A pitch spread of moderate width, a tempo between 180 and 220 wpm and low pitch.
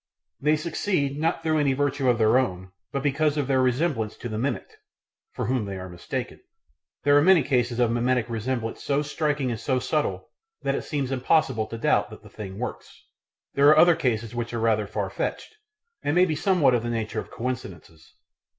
Yes: average, 4.4 semitones; average, 200 wpm; low, 130 Hz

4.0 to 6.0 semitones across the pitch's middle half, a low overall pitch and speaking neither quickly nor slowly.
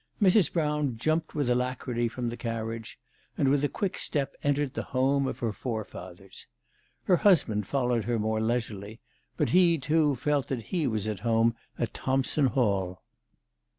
Yes: average, 4.5 semitones; low, 125 Hz; average, 160 wpm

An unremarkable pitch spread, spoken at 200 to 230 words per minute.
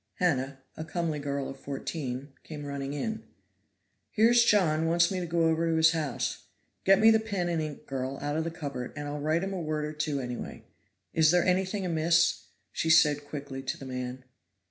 Yes: average, 3.4 semitones; fast, 205 wpm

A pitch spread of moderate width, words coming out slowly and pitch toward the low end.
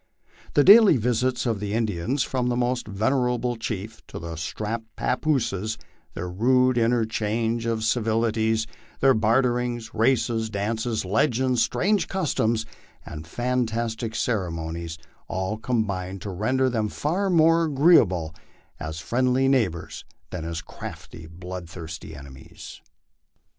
Yes: average, 4.5 semitones; slow, 120 wpm; low, 115 Hz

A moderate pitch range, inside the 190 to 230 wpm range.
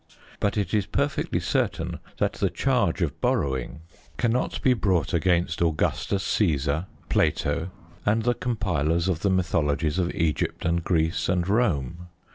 No: average, 4.2 semitones; average, 140 wpm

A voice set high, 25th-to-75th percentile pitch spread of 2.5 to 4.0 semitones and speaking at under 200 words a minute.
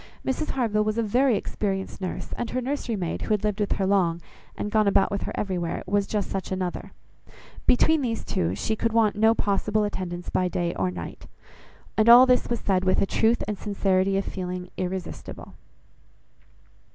Yes: high, 200 Hz; average, 3.1 semitones; average, 190 wpm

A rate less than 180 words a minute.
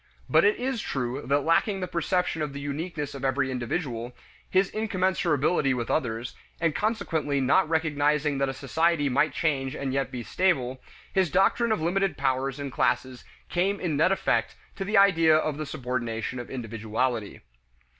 Yes: average, 165 wpm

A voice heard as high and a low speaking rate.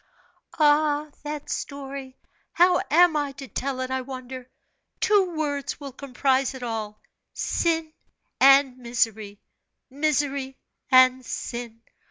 Yes: very high, 270 Hz; slow, 115 wpm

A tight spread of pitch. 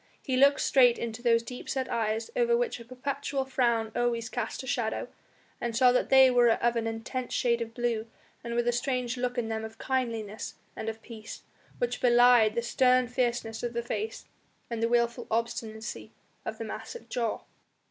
Yes: narrow, 1.9 semitones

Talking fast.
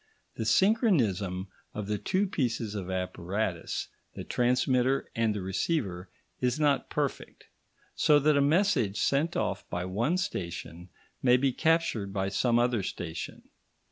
No: average, 140 wpm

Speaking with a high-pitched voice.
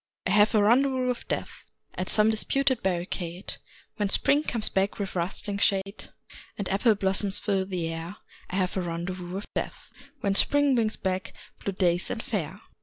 Yes: high, 195 Hz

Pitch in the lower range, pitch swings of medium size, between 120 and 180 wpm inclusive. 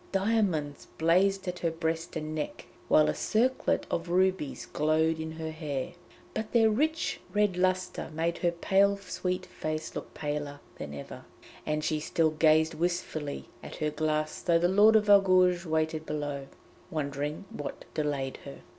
No: medium, 160 Hz; average, 3.3 semitones; average, 155 wpm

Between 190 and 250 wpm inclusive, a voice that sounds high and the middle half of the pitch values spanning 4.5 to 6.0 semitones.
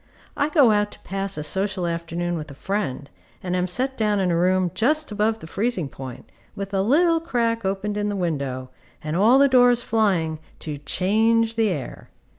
Yes: average, 195 wpm; high, 195 Hz; average, 5.0 semitones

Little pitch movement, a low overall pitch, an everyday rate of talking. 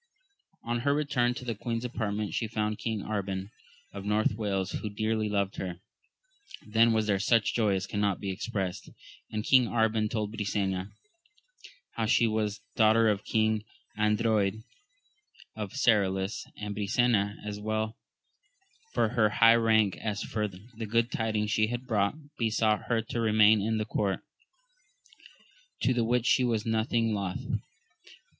Yes: narrow, 1.8 semitones; low, 110 Hz; average, 150 wpm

